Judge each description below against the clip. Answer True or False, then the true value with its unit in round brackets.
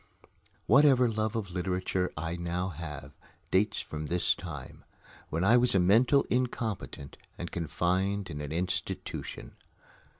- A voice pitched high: False (90 Hz)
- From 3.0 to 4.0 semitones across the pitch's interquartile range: False (4.5 semitones)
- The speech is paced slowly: True (130 wpm)